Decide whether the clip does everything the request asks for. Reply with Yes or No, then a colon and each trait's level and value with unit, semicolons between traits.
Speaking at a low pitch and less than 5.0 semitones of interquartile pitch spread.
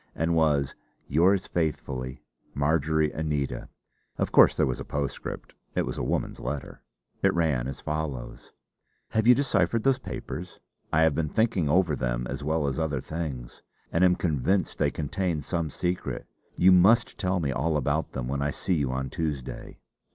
Yes: very low, 80 Hz; average, 4.2 semitones